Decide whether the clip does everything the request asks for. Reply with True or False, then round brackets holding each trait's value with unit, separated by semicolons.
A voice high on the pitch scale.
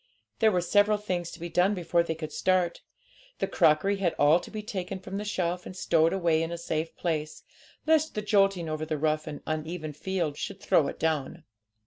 False (170 Hz)